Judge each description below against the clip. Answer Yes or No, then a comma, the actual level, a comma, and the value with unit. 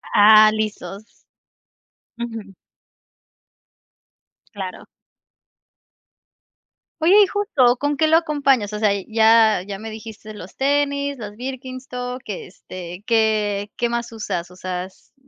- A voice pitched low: No, high, 220 Hz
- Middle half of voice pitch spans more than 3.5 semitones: Yes, average, 4.0 semitones